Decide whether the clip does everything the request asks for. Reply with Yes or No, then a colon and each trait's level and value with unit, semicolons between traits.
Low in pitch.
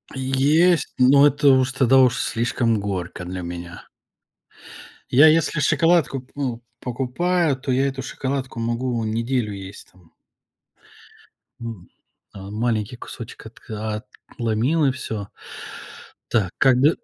Yes: low, 125 Hz